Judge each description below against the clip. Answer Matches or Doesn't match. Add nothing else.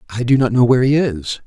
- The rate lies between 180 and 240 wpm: Doesn't match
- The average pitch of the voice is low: Matches